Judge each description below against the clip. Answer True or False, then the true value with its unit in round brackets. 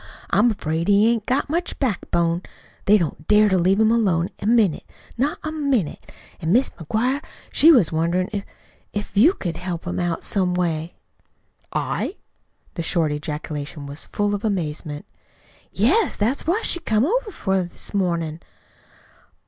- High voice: True (195 Hz)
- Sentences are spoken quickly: False (155 wpm)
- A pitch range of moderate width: False (5.9 semitones)